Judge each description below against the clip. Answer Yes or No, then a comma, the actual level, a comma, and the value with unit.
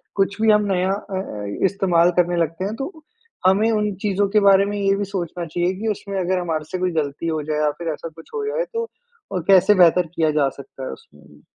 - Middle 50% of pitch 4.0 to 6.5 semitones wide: No, average, 3.6 semitones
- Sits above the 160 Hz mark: Yes, high, 190 Hz